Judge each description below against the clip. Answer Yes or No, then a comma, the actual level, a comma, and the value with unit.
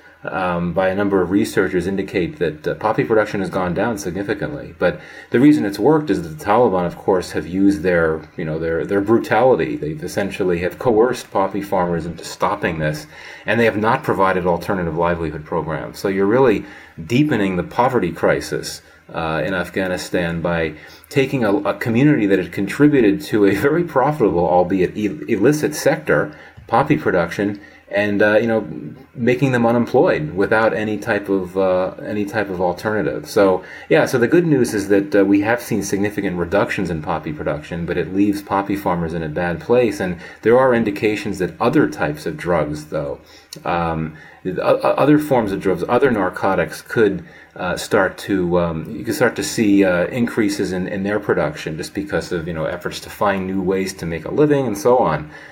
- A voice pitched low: Yes, low, 100 Hz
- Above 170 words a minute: Yes, average, 185 wpm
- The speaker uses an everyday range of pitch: Yes, average, 3.4 semitones